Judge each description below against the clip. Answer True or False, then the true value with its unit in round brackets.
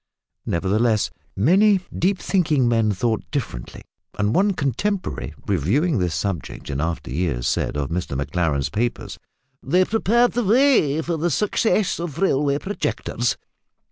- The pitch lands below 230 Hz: True (135 Hz)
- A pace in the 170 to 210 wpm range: False (140 wpm)